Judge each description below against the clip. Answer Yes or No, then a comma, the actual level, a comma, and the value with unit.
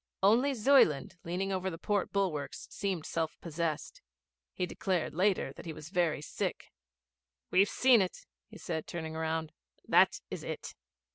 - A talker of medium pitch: Yes, medium, 180 Hz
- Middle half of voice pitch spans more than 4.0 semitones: No, average, 3.7 semitones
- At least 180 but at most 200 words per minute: No, average, 150 wpm